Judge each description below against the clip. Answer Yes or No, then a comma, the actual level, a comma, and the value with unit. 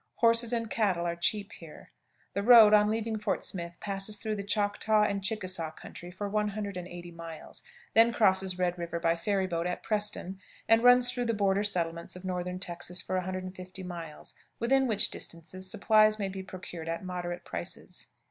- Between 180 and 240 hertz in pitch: Yes, high, 190 Hz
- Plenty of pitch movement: No, average, 3.3 semitones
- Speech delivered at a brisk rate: No, average, 175 wpm